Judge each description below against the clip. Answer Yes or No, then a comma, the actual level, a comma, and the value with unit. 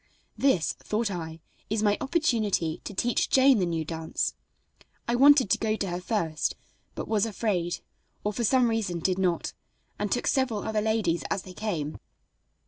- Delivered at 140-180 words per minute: Yes, average, 170 wpm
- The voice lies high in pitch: Yes, high, 210 Hz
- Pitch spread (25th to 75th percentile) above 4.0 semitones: Yes, average, 4.6 semitones